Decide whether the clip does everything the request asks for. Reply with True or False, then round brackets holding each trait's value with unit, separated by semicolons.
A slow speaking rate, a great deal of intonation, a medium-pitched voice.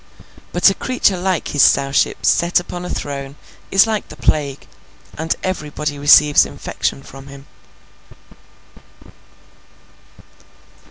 False (110 wpm; 4.3 semitones; 150 Hz)